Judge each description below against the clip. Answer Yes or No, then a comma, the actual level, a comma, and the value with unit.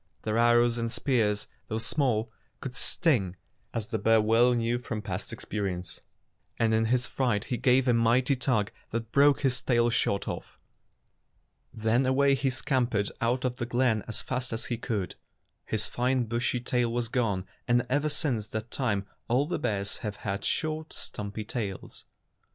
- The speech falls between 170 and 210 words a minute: Yes, average, 175 wpm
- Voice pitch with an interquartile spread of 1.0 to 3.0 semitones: Yes, average, 2.7 semitones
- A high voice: No, low, 120 Hz